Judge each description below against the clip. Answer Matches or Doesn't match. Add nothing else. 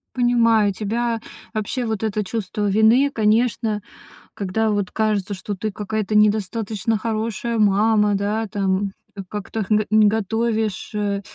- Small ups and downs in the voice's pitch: Matches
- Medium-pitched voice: Doesn't match